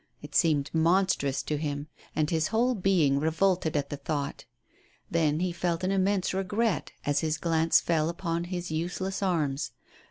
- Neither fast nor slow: Yes, average, 165 wpm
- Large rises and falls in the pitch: No, average, 3.5 semitones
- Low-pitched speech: No, medium, 165 Hz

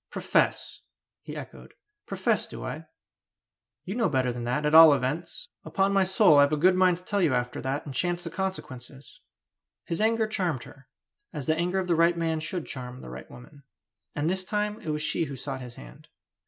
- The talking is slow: No, fast, 205 wpm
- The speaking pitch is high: No, medium, 160 Hz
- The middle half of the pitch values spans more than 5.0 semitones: Yes, wide, 5.4 semitones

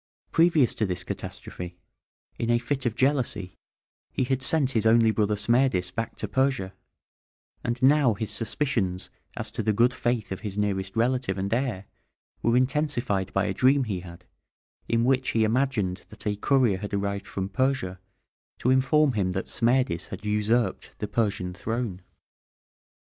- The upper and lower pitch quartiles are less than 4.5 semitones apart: No, average, 4.8 semitones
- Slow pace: No, average, 160 wpm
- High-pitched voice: No, low, 115 Hz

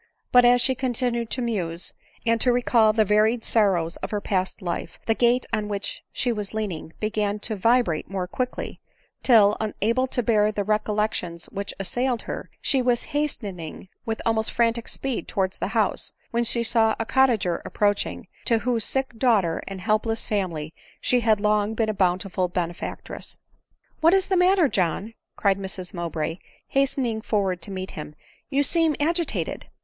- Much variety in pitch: No, average, 3.9 semitones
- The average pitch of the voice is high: Yes, high, 220 Hz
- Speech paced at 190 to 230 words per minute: No, average, 180 wpm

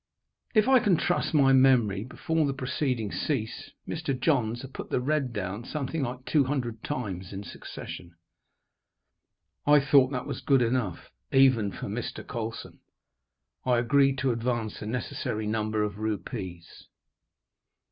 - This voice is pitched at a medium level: No, low, 125 Hz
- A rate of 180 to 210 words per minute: No, average, 145 wpm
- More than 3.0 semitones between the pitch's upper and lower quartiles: Yes, average, 4.1 semitones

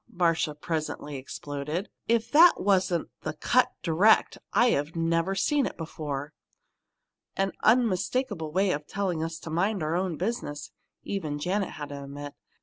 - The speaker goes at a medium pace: Yes, average, 145 wpm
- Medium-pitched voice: Yes, medium, 170 Hz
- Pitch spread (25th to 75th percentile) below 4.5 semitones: No, average, 4.8 semitones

